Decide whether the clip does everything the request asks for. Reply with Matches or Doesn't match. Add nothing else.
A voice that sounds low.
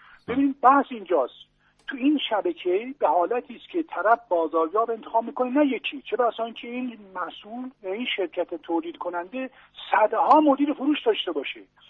Doesn't match